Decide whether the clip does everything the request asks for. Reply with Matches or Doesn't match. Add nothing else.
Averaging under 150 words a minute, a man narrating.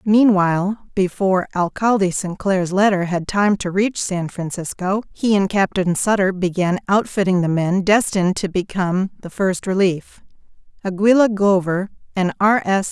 Doesn't match